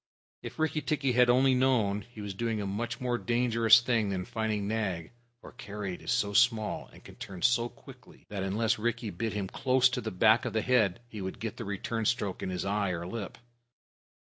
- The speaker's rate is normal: No, fast, 215 wpm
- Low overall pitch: Yes, low, 110 Hz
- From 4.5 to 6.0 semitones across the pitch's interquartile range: No, average, 3.2 semitones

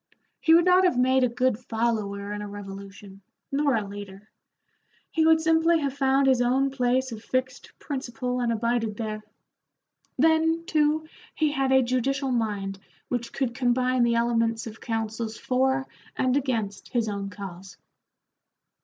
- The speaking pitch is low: No, high, 245 Hz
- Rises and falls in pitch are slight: No, average, 3.8 semitones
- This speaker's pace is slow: No, average, 155 wpm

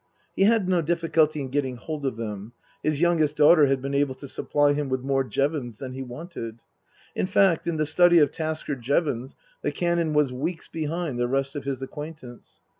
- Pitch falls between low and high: Yes, medium, 145 Hz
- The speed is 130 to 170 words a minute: No, average, 195 wpm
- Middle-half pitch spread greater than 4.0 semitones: No, average, 3.6 semitones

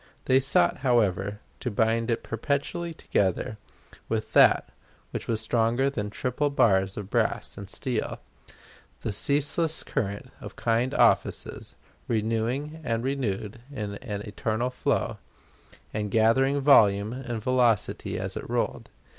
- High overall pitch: No, low, 115 Hz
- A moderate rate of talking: No, slow, 130 wpm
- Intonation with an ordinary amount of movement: Yes, average, 4.2 semitones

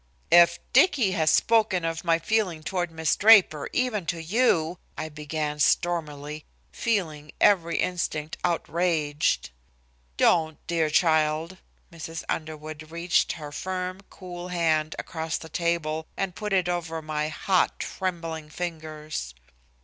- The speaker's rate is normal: No, slow, 125 wpm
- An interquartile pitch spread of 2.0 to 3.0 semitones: Yes, narrow, 2.5 semitones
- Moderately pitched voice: Yes, medium, 165 Hz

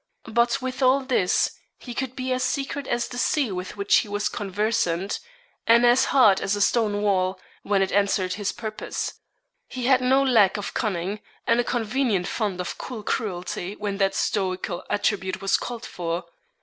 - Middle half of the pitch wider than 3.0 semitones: Yes, average, 4.4 semitones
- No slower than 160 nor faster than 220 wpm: Yes, average, 175 wpm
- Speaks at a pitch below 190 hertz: No, high, 210 Hz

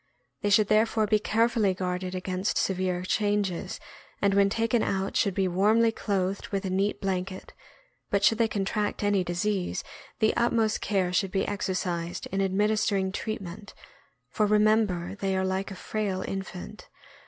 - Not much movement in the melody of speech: Yes, narrow, 2.2 semitones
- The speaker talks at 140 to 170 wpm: Yes, average, 160 wpm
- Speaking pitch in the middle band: No, high, 195 Hz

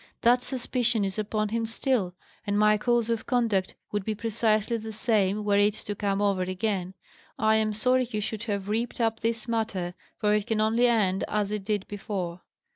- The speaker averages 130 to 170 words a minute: No, average, 195 wpm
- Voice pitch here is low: No, high, 215 Hz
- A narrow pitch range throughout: Yes, narrow, 2.1 semitones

